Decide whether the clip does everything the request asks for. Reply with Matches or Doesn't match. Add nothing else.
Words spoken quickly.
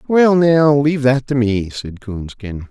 Doesn't match